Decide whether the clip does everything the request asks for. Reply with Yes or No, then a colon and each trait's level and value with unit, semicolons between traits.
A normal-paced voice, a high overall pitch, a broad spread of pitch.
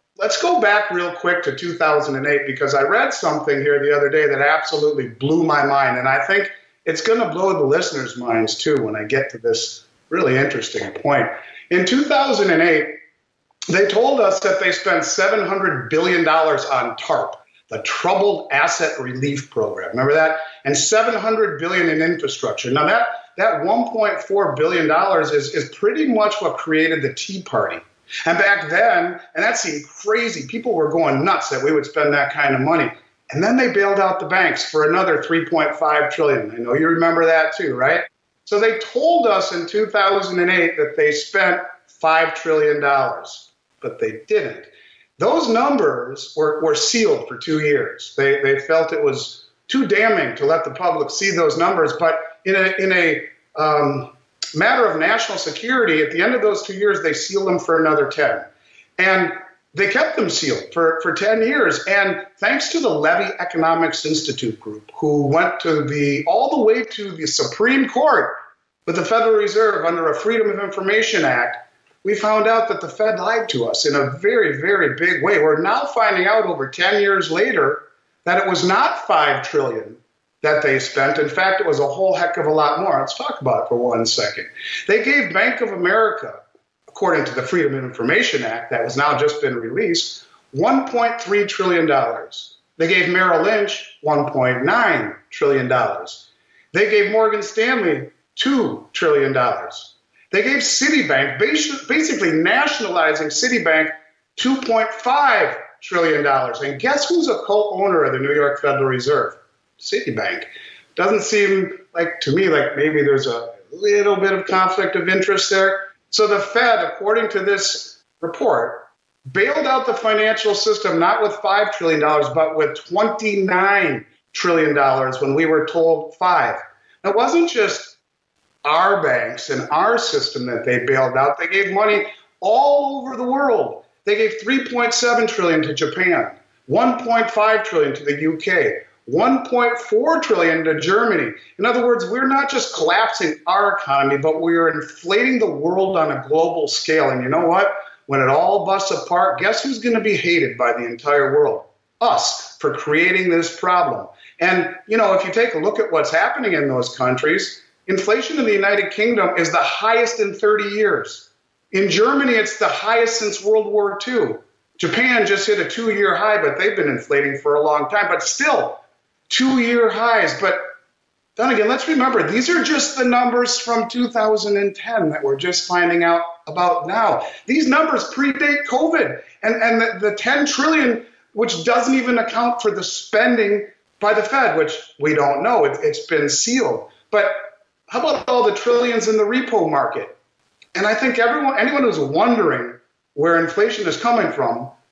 Yes: average, 170 wpm; high, 205 Hz; wide, 6.9 semitones